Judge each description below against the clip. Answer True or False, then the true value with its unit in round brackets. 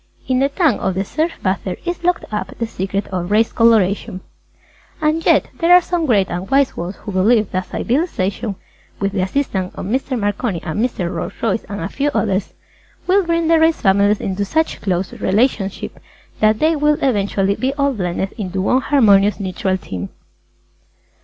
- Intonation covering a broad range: True (6.6 semitones)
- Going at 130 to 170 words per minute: False (185 wpm)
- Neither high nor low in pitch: False (210 Hz)